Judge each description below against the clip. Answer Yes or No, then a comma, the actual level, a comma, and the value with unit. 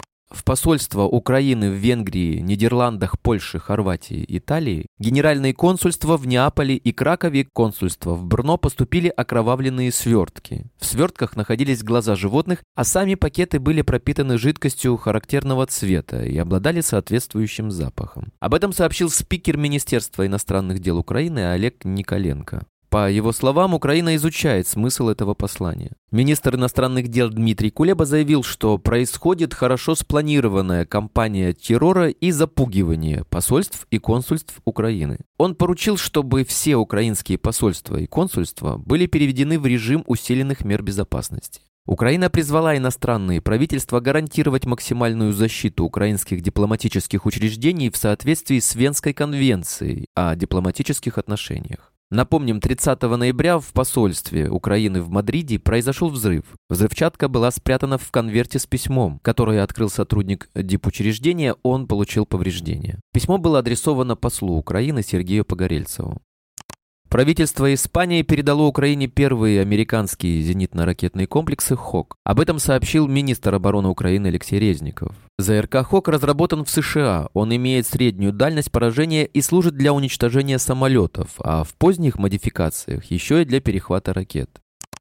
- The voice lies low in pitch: Yes, low, 120 Hz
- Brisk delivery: No, average, 125 wpm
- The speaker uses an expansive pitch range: Yes, wide, 6.2 semitones